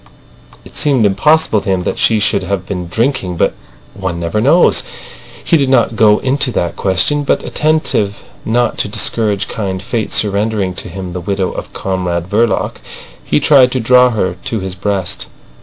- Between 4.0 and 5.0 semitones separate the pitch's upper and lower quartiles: Yes, average, 4.6 semitones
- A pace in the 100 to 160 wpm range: No, average, 175 wpm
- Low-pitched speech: Yes, low, 105 Hz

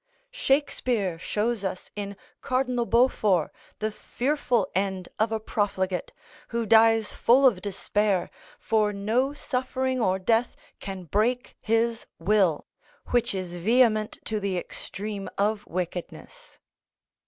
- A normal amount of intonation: Yes, average, 3.8 semitones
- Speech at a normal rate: No, slow, 120 wpm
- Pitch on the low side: No, high, 215 Hz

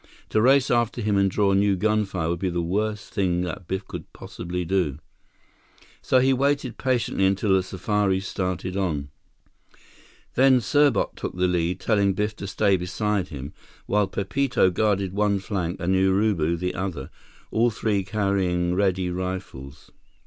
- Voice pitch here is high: No, very low, 95 Hz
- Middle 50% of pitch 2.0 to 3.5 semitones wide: Yes, average, 2.7 semitones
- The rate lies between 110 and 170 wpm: Yes, average, 155 wpm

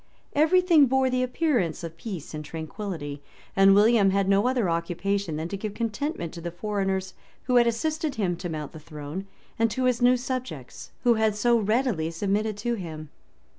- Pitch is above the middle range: Yes, high, 200 Hz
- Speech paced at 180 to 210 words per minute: Yes, average, 190 wpm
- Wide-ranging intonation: Yes, wide, 6.4 semitones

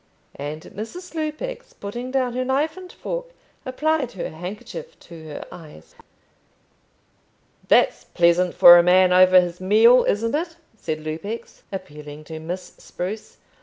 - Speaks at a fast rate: No, slow, 135 wpm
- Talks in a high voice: Yes, high, 195 Hz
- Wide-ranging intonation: Yes, wide, 7.5 semitones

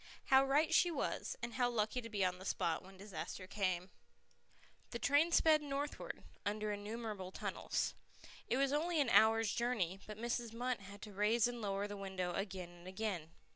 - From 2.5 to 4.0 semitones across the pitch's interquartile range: No, average, 4.4 semitones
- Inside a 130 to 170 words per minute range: No, average, 185 wpm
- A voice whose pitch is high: Yes, high, 215 Hz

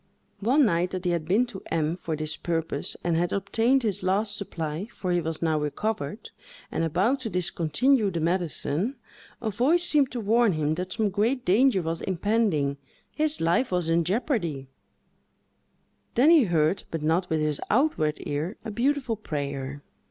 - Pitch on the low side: No, medium, 180 Hz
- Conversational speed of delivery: Yes, average, 170 wpm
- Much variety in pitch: Yes, wide, 5.9 semitones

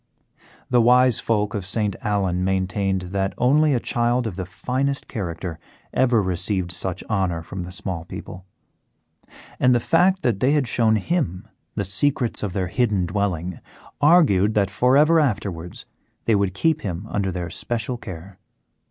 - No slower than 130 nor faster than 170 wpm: Yes, average, 160 wpm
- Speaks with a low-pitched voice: Yes, low, 100 Hz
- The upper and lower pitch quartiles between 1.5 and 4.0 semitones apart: No, average, 5.1 semitones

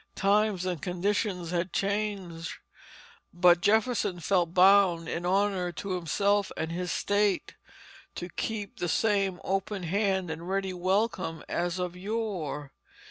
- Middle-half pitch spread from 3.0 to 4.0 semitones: No, narrow, 2.5 semitones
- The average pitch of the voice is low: No, medium, 185 Hz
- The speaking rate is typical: No, slow, 130 wpm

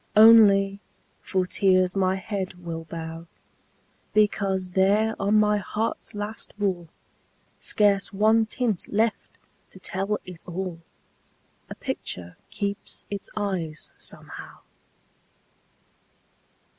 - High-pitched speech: Yes, high, 195 Hz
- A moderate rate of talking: No, slow, 100 wpm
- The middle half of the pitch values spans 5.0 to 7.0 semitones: No, narrow, 2.4 semitones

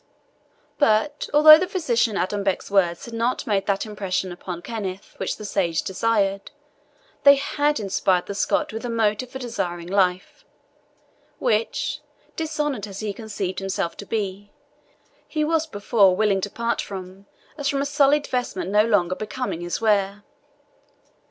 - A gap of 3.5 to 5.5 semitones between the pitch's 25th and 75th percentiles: Yes, average, 4.3 semitones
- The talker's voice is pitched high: Yes, high, 210 Hz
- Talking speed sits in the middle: Yes, average, 150 wpm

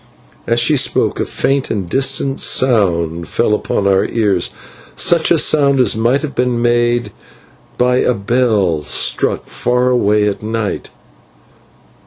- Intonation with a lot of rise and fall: No, average, 3.8 semitones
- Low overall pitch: Yes, low, 120 Hz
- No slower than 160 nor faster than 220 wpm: No, average, 140 wpm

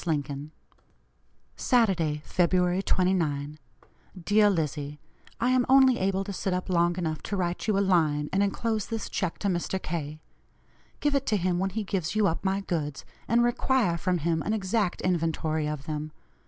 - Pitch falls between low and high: Yes, medium, 180 Hz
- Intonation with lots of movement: No, average, 4.3 semitones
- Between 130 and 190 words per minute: Yes, average, 170 wpm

